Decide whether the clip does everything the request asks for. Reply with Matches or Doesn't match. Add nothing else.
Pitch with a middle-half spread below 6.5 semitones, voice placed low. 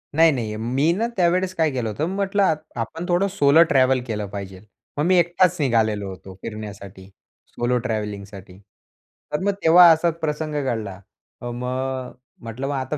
Doesn't match